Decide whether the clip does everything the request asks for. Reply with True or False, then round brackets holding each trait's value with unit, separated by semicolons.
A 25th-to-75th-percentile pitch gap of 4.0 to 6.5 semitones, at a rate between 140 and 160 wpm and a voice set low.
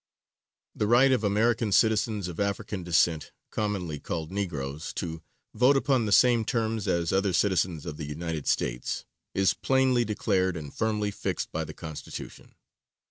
True (5.1 semitones; 155 wpm; 100 Hz)